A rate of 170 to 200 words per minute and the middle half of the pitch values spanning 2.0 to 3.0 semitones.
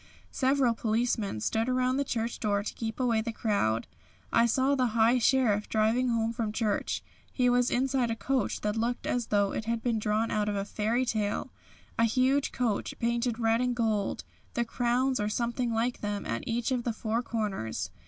Yes: average, 195 wpm; narrow, 2.4 semitones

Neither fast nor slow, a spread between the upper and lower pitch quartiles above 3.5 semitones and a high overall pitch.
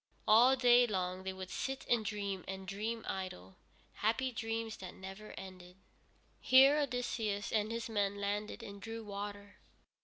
No: average, 150 wpm; average, 3.1 semitones; high, 210 Hz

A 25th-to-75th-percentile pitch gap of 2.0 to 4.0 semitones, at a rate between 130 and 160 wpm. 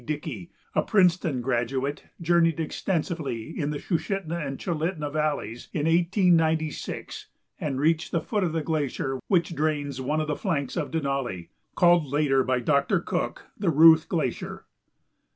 Yes: average, 3.4 semitones; average, 145 wpm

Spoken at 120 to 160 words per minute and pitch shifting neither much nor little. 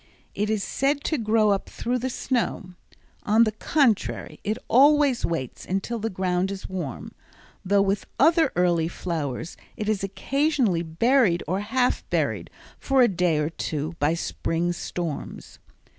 No: average, 150 wpm; wide, 6.0 semitones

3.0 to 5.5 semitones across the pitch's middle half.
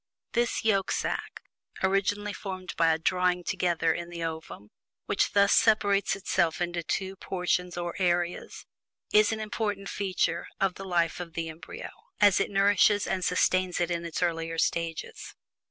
No: narrow, 2.6 semitones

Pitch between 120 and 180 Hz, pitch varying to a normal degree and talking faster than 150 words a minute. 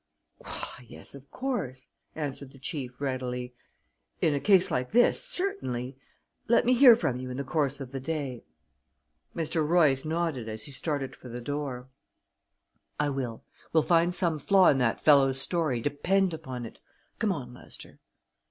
Yes: medium, 140 Hz; average, 4.7 semitones; average, 160 wpm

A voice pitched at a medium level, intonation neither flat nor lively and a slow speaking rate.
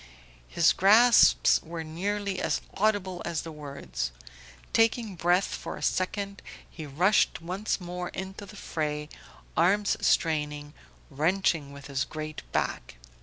Yes: medium, 175 Hz; average, 4.7 semitones; slow, 125 wpm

